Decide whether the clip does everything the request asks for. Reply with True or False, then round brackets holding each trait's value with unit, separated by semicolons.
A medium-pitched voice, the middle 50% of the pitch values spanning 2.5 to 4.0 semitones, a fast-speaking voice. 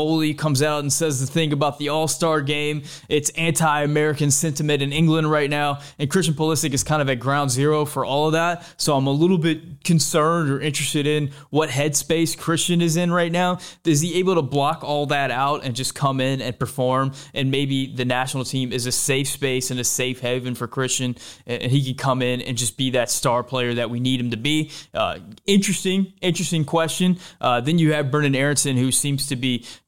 True (145 Hz; 3.2 semitones; 215 wpm)